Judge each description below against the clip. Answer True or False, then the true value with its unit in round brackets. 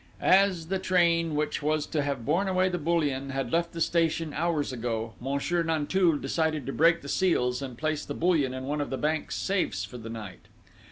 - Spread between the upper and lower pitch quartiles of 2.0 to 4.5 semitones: True (3.8 semitones)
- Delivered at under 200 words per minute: False (205 wpm)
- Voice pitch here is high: False (155 Hz)